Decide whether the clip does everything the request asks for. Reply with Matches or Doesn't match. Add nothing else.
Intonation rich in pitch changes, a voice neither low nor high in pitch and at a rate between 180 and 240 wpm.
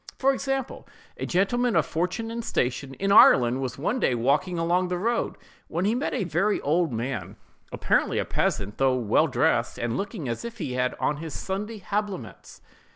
Matches